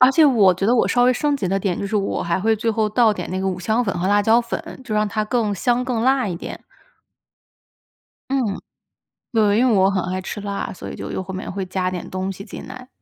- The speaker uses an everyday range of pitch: Yes, average, 4.1 semitones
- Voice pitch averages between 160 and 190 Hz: No, high, 210 Hz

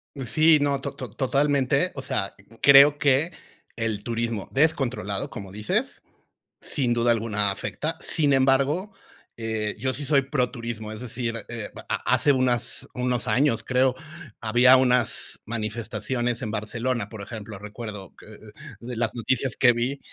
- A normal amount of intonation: Yes, average, 3.6 semitones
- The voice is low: Yes, low, 120 Hz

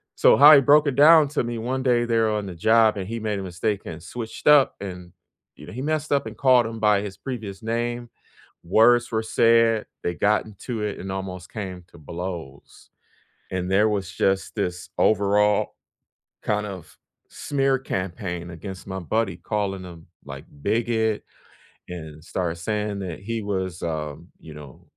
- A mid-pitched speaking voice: No, low, 105 Hz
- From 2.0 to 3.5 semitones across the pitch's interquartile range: No, average, 4.1 semitones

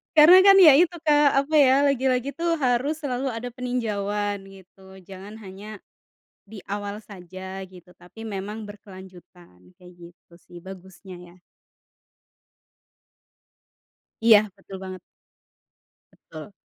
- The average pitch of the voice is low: No, high, 205 Hz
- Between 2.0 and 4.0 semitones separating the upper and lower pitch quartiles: No, average, 4.8 semitones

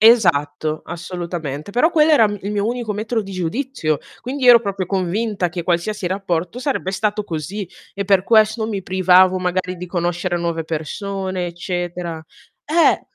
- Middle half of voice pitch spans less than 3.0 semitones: No, average, 3.7 semitones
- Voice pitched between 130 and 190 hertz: Yes, medium, 185 Hz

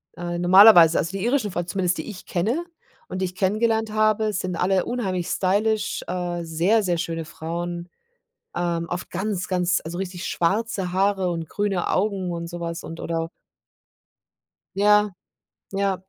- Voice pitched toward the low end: No, medium, 185 Hz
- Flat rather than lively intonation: No, average, 3.1 semitones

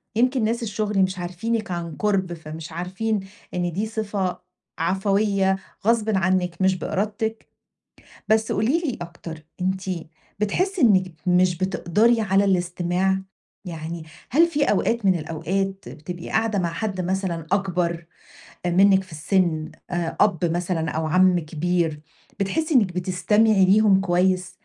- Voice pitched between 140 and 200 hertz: Yes, high, 190 Hz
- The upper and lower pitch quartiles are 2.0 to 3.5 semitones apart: Yes, average, 3.2 semitones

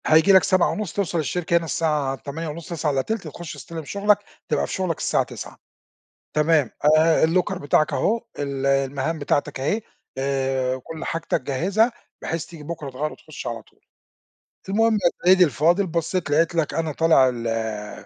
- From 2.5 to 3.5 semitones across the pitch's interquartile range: No, average, 4.0 semitones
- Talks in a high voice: No, medium, 160 Hz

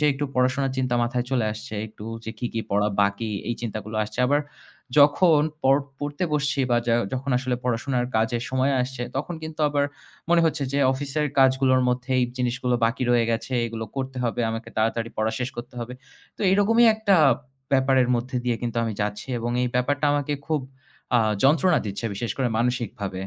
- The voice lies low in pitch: Yes, low, 125 Hz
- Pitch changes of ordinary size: Yes, average, 3.2 semitones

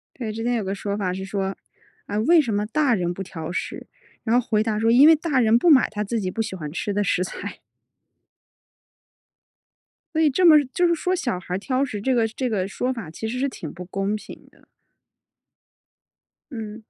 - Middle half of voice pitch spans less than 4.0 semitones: No, average, 4.7 semitones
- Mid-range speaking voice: No, high, 220 Hz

